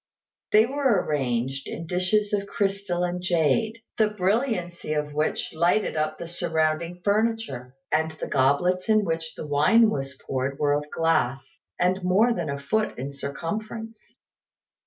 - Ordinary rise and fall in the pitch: No, wide, 6.1 semitones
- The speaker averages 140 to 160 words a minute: Yes, average, 150 wpm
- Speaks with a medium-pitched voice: Yes, medium, 175 Hz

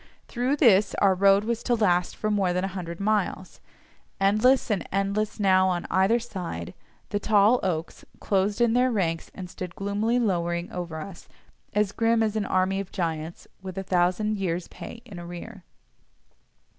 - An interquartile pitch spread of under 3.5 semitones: Yes, average, 3.0 semitones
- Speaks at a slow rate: No, average, 170 wpm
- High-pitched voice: Yes, high, 195 Hz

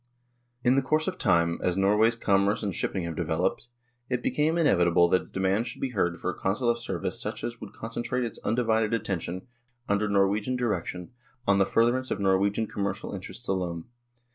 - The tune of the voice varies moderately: Yes, average, 3.9 semitones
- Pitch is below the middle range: Yes, low, 100 Hz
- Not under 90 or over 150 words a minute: No, average, 190 wpm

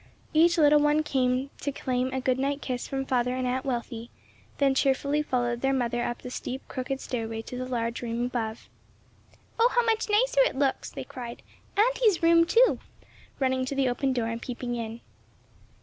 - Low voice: No, very high, 260 Hz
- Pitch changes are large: No, average, 3.1 semitones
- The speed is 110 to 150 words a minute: No, average, 185 wpm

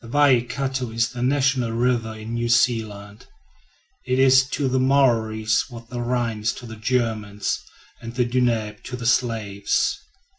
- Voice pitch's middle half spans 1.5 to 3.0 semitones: Yes, narrow, 2.4 semitones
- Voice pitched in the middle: No, low, 120 Hz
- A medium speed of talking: Yes, average, 155 wpm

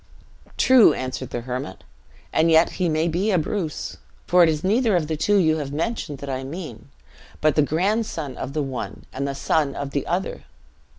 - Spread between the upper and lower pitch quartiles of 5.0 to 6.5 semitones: No, average, 4.5 semitones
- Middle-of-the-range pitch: Yes, medium, 155 Hz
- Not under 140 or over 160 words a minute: No, average, 195 wpm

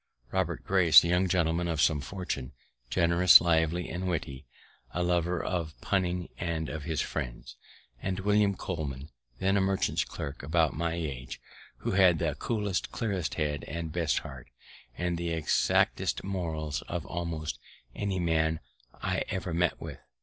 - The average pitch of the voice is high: No, very low, 85 Hz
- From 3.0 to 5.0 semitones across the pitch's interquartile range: No, narrow, 2.6 semitones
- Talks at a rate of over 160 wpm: No, average, 150 wpm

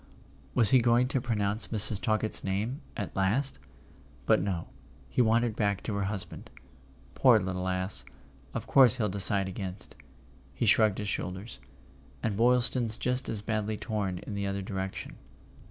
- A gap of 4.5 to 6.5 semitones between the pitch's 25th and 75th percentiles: No, average, 3.3 semitones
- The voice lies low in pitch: Yes, low, 105 Hz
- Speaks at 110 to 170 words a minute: Yes, average, 155 wpm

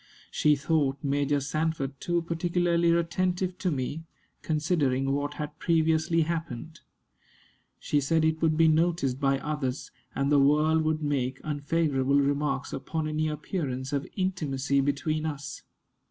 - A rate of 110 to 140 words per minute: Yes, slow, 135 wpm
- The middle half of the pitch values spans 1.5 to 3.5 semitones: Yes, average, 2.7 semitones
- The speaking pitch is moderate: Yes, medium, 150 Hz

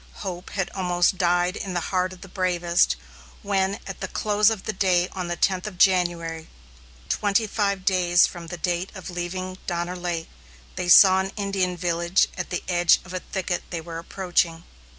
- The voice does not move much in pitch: Yes, narrow, 1.5 semitones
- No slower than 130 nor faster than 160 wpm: No, average, 180 wpm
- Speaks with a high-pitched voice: No, medium, 180 Hz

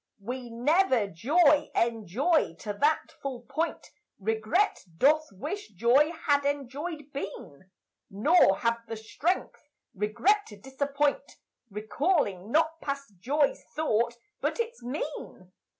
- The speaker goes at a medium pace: No, slow, 115 wpm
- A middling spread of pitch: No, wide, 6.0 semitones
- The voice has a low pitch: No, very high, 275 Hz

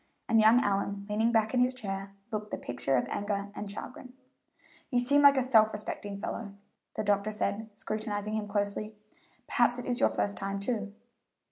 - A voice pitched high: Yes, high, 210 Hz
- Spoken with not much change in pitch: Yes, narrow, 2.3 semitones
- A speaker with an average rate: Yes, average, 180 wpm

